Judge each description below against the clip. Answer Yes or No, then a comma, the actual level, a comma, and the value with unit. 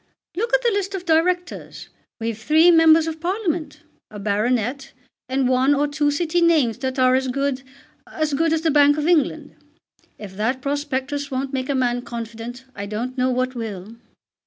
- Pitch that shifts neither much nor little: Yes, average, 4.3 semitones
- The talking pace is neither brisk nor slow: Yes, average, 180 wpm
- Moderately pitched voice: No, very high, 275 Hz